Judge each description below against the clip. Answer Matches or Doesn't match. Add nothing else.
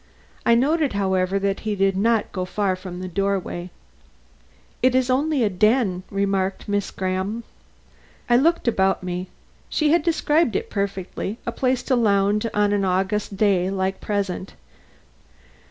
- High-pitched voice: Matches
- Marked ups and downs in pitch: Doesn't match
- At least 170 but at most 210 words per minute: Doesn't match